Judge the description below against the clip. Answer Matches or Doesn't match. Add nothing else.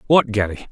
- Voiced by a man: Matches